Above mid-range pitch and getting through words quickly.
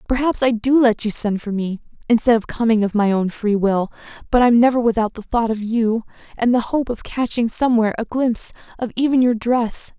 Yes: high, 230 Hz; fast, 215 wpm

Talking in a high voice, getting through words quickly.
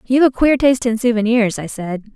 Yes: high, 235 Hz; fast, 225 wpm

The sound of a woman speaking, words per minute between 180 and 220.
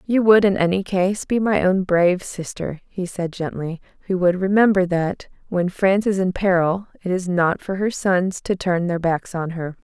Yes: female; fast, 205 wpm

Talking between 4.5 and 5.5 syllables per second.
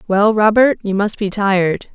Yes: 4.6 syllables/s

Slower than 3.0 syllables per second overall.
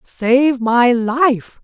Yes: 2.0 syllables/s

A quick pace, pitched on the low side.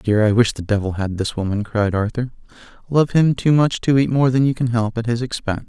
Yes: fast, 265 wpm; low, 115 Hz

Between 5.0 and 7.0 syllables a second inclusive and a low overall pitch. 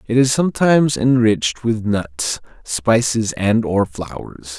No: 4.0 syllables/s; low, 110 Hz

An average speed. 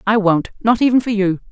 No: fast, 235 wpm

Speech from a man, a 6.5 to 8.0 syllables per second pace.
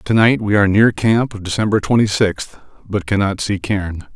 No: male; 5.0 syllables/s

